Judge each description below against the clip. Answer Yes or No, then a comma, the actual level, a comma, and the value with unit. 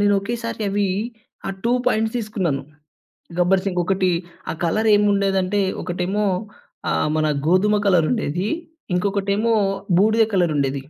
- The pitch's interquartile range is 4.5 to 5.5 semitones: No, average, 2.8 semitones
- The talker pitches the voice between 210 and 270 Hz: No, high, 195 Hz